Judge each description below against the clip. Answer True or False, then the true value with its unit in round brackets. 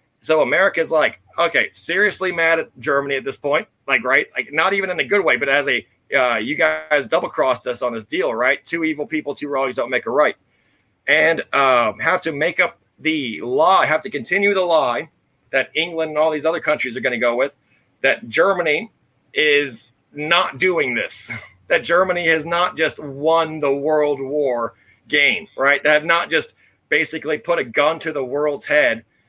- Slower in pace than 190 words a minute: False (195 wpm)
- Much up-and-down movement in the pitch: False (3.7 semitones)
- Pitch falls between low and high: True (155 Hz)